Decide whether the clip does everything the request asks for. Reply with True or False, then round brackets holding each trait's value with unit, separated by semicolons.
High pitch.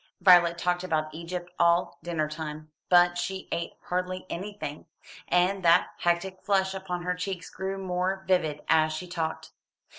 False (180 Hz)